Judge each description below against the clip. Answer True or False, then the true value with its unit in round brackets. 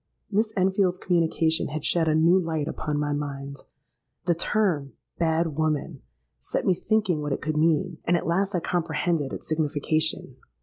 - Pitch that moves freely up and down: False (2.9 semitones)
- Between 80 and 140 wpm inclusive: False (165 wpm)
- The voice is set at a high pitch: False (160 Hz)